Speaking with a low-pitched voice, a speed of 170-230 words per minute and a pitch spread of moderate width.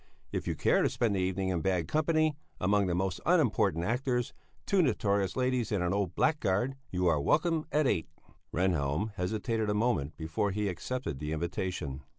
No: low, 100 Hz; average, 175 wpm; wide, 5.8 semitones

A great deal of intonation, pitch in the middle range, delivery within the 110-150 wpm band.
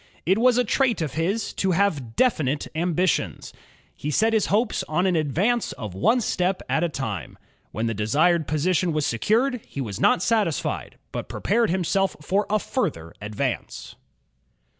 No: wide, 6.7 semitones; medium, 175 Hz; average, 160 wpm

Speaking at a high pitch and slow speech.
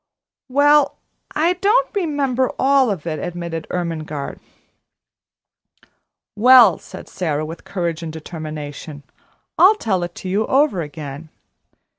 No: medium, 180 Hz; slow, 115 wpm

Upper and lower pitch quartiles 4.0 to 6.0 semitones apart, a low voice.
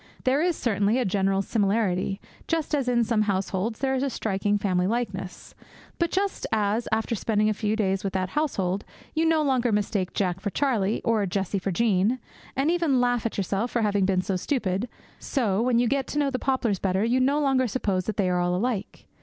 No: average, 4.8 semitones; high, 215 Hz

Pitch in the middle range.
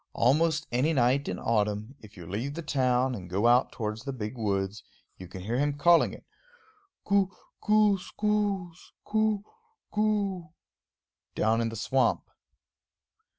No: low, 130 Hz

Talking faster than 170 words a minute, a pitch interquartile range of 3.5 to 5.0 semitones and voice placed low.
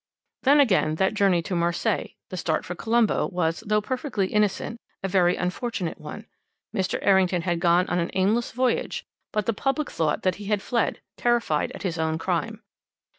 No: average, 180 wpm; average, 4.2 semitones; high, 190 Hz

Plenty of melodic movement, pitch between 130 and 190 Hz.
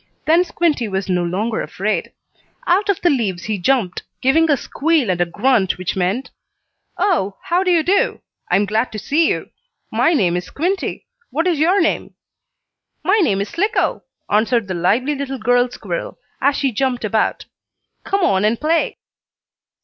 No: wide, 8.6 semitones; very high, 250 Hz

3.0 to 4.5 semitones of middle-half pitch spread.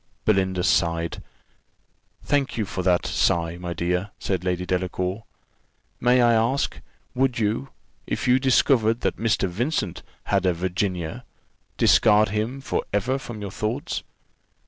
No: average, 4.9 semitones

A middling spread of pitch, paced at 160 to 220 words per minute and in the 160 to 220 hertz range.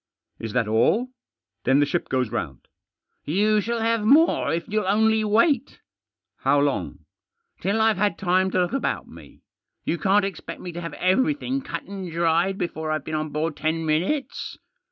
No: wide, 5.7 semitones; average, 185 wpm; high, 190 Hz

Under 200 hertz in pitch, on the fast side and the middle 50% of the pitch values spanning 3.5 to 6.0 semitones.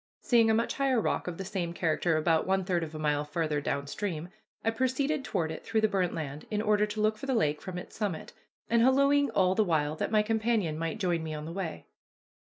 Yes: high, 190 Hz; fast, 240 wpm; wide, 5.6 semitones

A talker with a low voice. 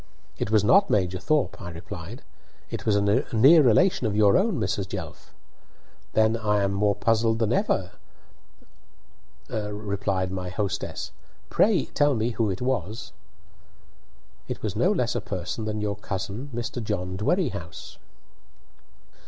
Yes: low, 105 Hz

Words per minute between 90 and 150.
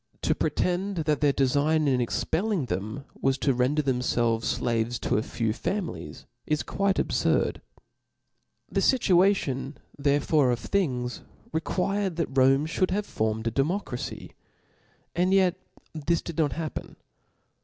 Yes: average, 145 wpm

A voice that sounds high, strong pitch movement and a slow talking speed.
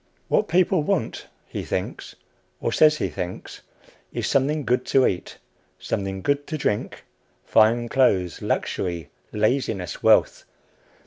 No: low, 125 Hz; wide, 7.3 semitones; slow, 125 wpm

